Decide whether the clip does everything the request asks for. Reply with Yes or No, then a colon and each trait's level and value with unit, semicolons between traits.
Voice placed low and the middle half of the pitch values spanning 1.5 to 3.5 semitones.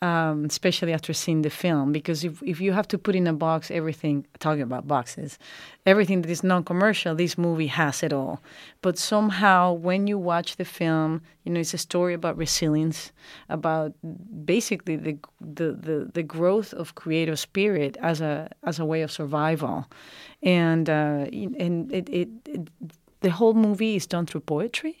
No: medium, 165 Hz; narrow, 2.6 semitones